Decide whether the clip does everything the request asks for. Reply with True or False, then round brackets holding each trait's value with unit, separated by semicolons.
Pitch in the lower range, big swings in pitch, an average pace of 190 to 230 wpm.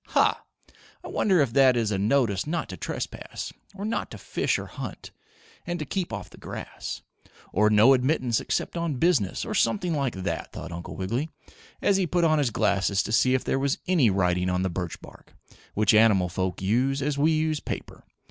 True (125 Hz; 7.8 semitones; 200 wpm)